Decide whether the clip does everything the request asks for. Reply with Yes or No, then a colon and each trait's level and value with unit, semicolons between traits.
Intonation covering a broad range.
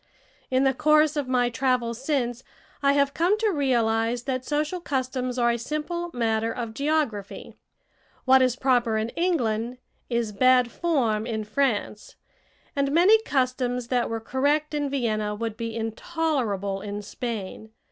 No: average, 4.0 semitones